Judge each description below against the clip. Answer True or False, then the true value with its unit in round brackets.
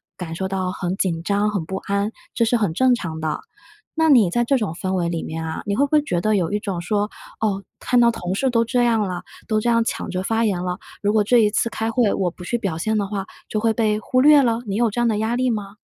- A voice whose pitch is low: False (210 Hz)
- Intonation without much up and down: False (3.8 semitones)